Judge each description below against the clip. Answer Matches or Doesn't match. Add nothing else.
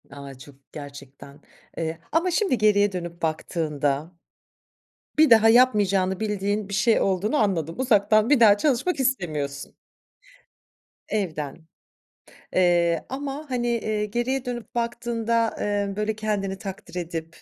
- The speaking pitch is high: Matches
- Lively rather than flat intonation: Matches